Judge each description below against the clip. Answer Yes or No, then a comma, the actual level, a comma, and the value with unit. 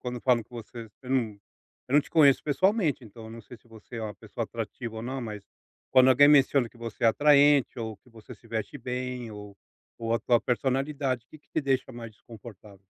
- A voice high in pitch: No, low, 120 Hz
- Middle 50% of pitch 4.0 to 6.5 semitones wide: No, average, 3.2 semitones